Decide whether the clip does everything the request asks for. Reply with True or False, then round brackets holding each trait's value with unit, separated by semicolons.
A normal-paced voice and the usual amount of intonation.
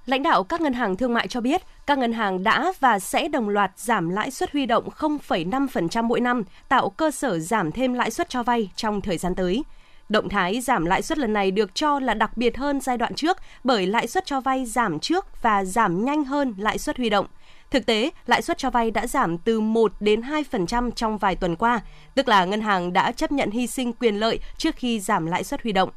True (240 wpm; 4.8 semitones)